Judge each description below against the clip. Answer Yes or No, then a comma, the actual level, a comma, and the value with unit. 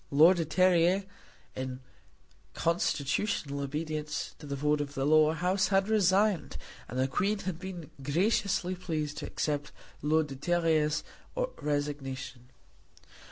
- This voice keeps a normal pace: No, slow, 125 wpm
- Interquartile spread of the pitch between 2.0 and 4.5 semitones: Yes, average, 4.1 semitones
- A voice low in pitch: No, medium, 155 Hz